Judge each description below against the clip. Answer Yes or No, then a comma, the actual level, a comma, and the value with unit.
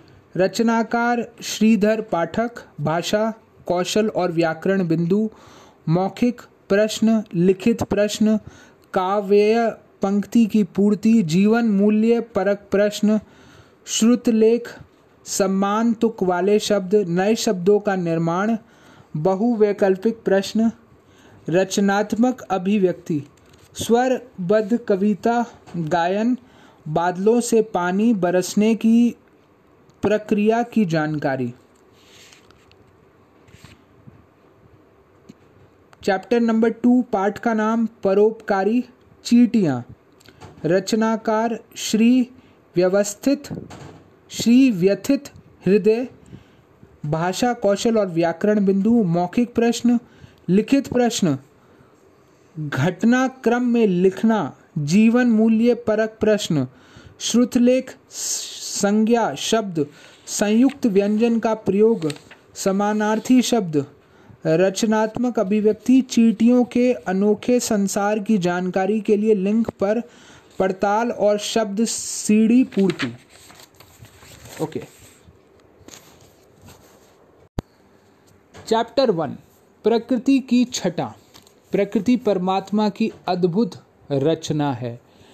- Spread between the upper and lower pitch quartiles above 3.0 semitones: Yes, average, 3.9 semitones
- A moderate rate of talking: No, slow, 80 wpm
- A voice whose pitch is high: Yes, high, 210 Hz